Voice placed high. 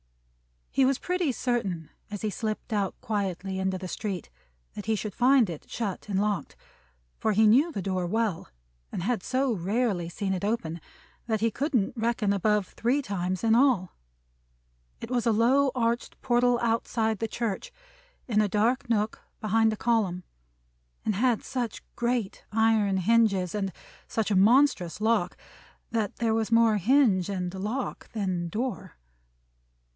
Yes: high, 220 Hz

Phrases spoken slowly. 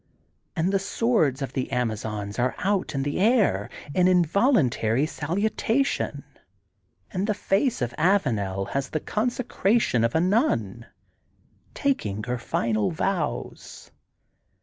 Yes: slow, 125 wpm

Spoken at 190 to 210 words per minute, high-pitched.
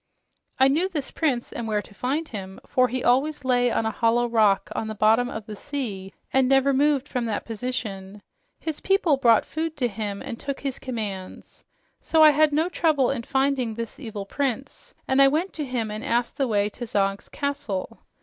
Yes: average, 200 wpm; very high, 250 Hz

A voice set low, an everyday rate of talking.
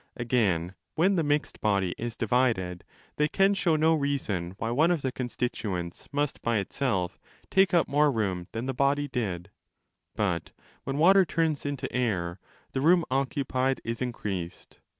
Yes: low, 125 Hz; average, 160 wpm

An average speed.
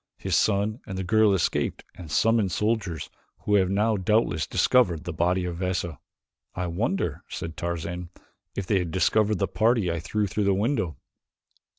Yes: average, 170 wpm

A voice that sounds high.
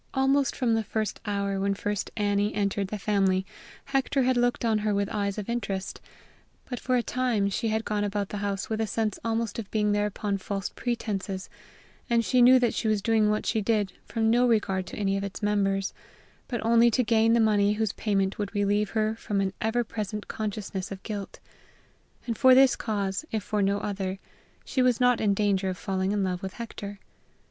Yes: high, 210 Hz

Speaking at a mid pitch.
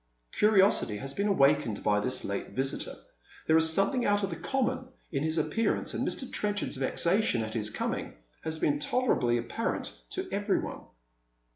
Yes: medium, 160 Hz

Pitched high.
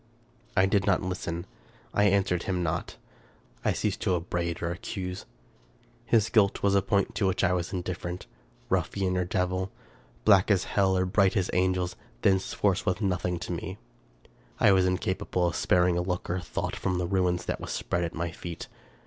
No: very low, 90 Hz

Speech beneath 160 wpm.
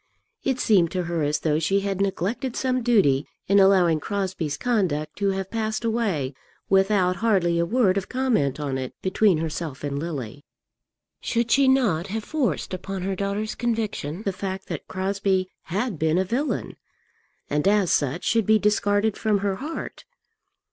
No: average, 165 wpm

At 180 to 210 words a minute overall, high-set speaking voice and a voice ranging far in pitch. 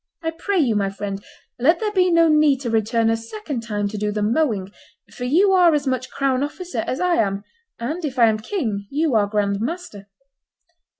Yes: fast, 205 wpm; very high, 250 Hz; wide, 7.4 semitones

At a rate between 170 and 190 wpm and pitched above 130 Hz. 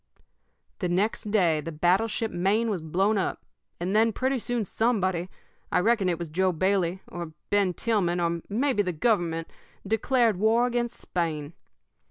No: average, 155 wpm; high, 190 Hz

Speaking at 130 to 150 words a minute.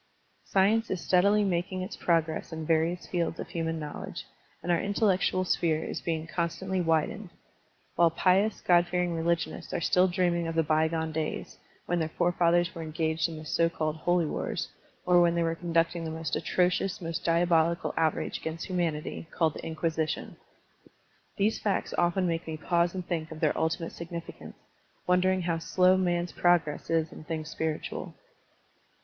No: average, 170 wpm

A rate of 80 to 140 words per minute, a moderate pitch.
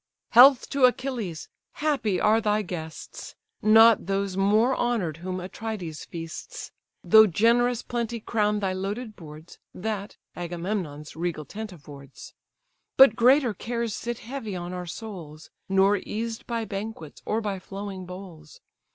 No: slow, 135 wpm; high, 205 Hz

